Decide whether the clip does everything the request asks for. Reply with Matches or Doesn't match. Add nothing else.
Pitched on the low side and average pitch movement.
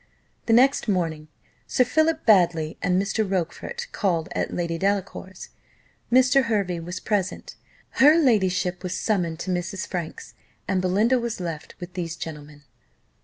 Doesn't match